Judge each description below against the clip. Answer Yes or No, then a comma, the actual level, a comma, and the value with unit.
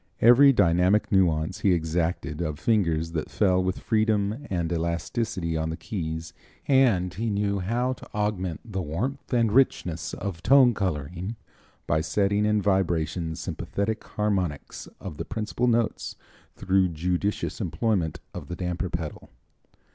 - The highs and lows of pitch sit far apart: No, average, 4.3 semitones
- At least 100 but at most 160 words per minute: Yes, average, 140 wpm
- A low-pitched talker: Yes, very low, 95 Hz